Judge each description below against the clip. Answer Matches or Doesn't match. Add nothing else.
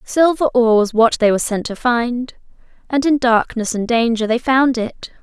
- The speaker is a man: Doesn't match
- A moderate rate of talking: Matches